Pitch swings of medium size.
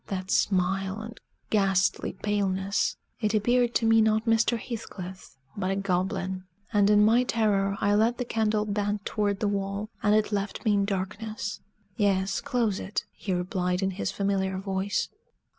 No: narrow, 2.0 semitones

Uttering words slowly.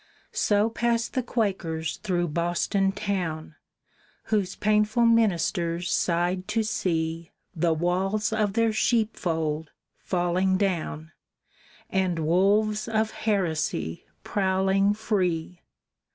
Yes: slow, 100 wpm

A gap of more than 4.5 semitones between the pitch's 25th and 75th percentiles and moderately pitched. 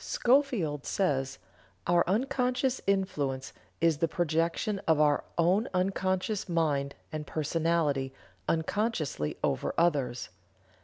Yes: average, 4.9 semitones; medium, 165 Hz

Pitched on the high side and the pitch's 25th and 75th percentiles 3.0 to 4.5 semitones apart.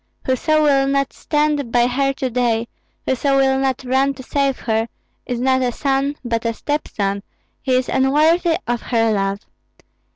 No: very high, 265 Hz; narrow, 2.6 semitones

